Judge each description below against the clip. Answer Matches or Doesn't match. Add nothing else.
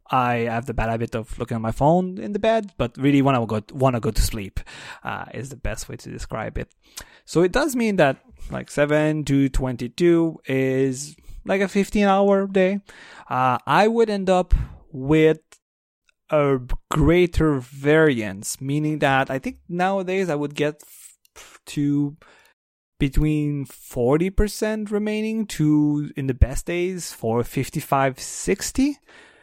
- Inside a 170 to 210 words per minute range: Doesn't match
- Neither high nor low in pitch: Matches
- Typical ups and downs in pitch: Doesn't match